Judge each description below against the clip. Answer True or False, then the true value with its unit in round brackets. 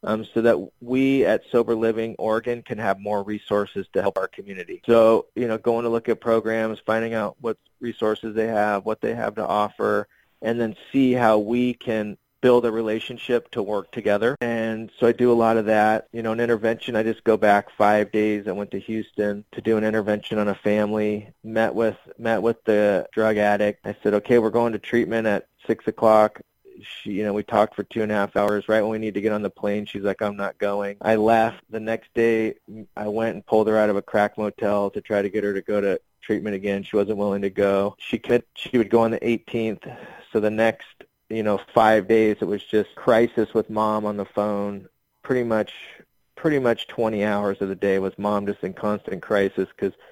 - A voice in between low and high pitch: False (110 Hz)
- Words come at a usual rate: False (225 wpm)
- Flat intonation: True (1.7 semitones)